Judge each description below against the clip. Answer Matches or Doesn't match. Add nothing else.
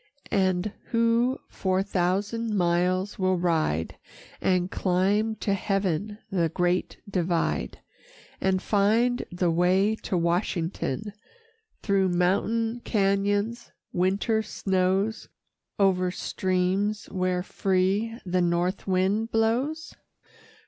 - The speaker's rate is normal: Doesn't match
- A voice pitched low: Doesn't match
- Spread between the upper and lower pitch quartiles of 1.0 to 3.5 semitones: Matches